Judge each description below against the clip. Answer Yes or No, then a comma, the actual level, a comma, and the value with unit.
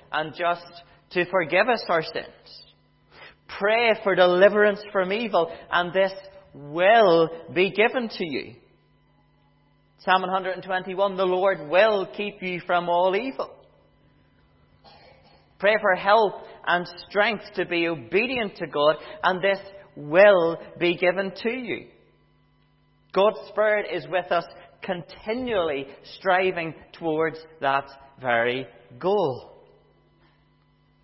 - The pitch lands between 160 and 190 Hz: Yes, medium, 185 Hz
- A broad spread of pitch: No, average, 3.4 semitones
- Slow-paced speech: Yes, slow, 110 wpm